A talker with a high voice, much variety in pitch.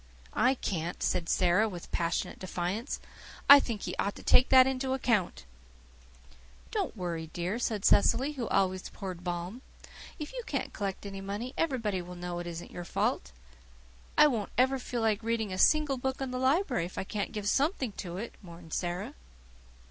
Yes: high, 205 Hz; wide, 6.3 semitones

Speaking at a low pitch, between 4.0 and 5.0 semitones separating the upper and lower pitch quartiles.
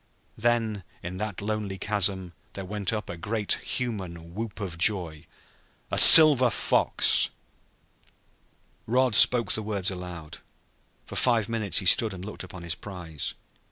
No: low, 100 Hz; average, 3.6 semitones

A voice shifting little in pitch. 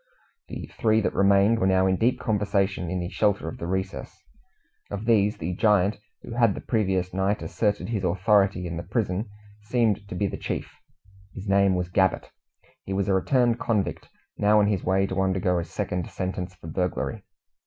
Yes: narrow, 2.2 semitones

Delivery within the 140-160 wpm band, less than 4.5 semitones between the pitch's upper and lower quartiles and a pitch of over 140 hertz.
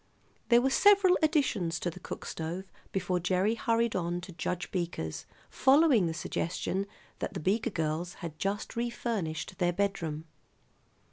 No: average, 145 wpm; average, 5.3 semitones; medium, 185 Hz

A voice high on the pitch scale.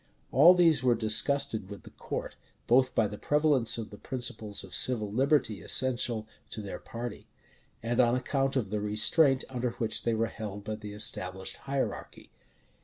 No: low, 115 Hz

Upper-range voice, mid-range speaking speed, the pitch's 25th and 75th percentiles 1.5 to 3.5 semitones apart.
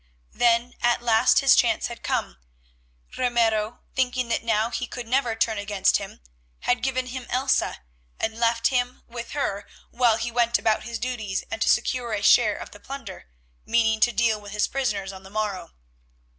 Yes: high, 235 Hz; average, 180 wpm; narrow, 2.4 semitones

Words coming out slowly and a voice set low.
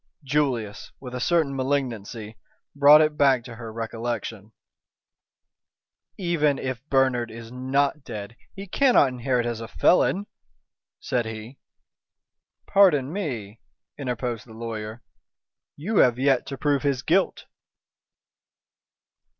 Yes: slow, 115 wpm; low, 130 Hz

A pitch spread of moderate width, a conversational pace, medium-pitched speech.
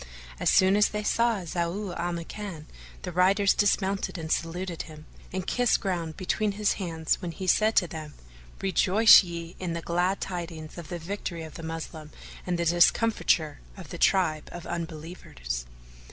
Yes: average, 3.0 semitones; average, 165 wpm; medium, 175 Hz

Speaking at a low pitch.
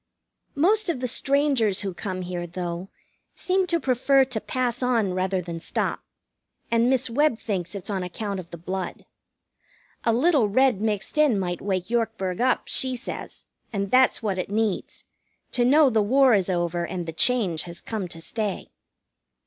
No: high, 215 Hz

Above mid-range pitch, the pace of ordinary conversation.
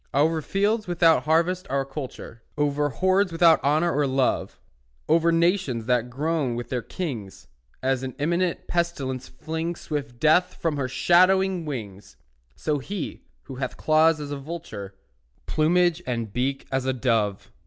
No: medium, 150 Hz; average, 150 wpm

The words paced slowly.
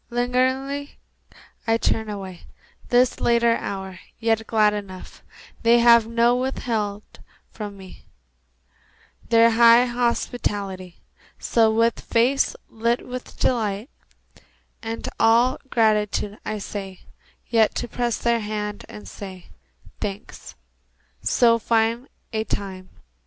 Yes: slow, 110 wpm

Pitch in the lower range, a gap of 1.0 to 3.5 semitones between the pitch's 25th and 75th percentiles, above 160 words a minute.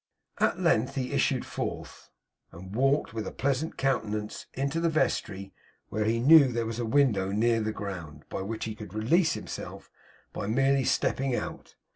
No: low, 115 Hz; average, 4.4 semitones; average, 170 wpm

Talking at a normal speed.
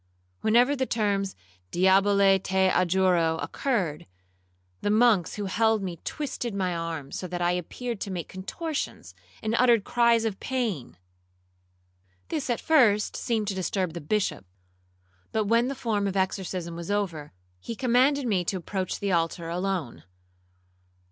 Yes: average, 145 wpm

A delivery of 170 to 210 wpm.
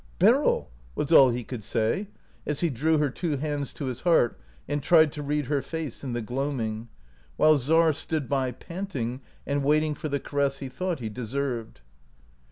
Yes: average, 195 wpm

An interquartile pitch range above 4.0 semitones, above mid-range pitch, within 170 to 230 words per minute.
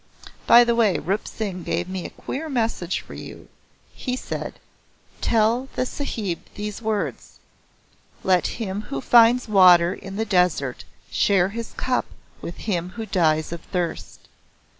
No: average, 4.5 semitones; high, 200 Hz; average, 145 wpm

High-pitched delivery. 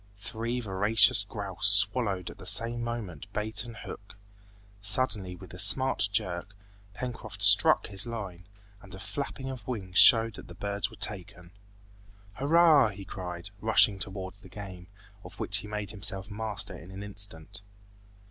No: low, 100 Hz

